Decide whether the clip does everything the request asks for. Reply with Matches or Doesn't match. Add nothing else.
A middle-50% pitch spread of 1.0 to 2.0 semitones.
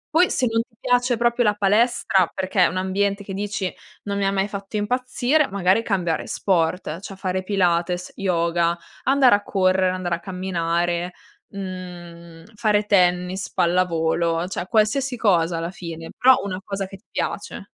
Doesn't match